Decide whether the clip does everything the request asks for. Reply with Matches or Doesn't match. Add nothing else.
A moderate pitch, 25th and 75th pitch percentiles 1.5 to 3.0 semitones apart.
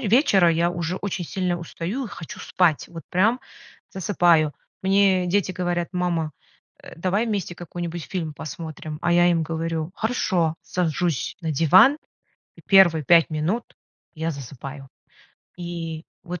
Matches